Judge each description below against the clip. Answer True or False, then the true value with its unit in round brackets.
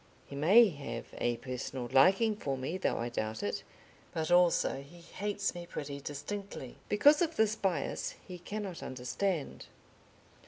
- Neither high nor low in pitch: True (170 Hz)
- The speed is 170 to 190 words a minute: False (150 wpm)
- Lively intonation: True (7.0 semitones)